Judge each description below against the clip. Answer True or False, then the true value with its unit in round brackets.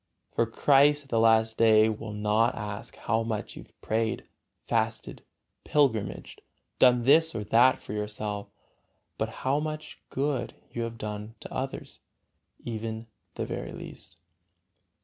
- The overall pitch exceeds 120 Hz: False (115 Hz)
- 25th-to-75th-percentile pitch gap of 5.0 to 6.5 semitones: False (3.2 semitones)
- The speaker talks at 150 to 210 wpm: False (140 wpm)